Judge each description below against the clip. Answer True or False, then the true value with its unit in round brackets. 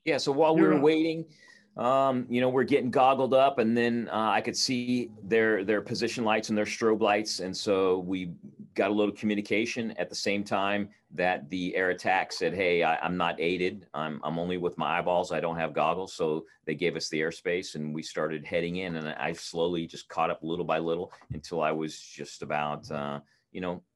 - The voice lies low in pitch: True (95 Hz)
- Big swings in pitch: True (6.0 semitones)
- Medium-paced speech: False (215 wpm)